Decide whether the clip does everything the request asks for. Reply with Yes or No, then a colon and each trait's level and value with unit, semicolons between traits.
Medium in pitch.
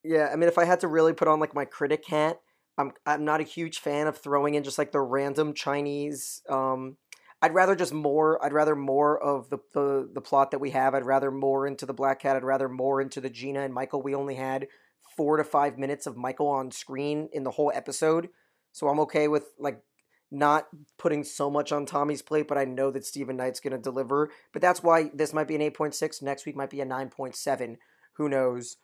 Yes: medium, 145 Hz